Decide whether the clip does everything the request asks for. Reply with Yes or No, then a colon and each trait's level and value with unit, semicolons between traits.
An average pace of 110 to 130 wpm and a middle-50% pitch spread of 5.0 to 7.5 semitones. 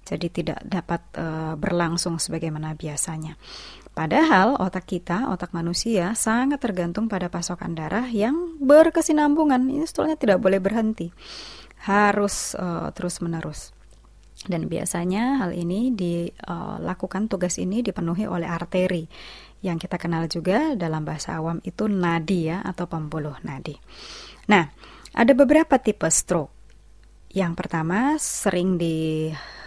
No: average, 120 wpm; average, 4.2 semitones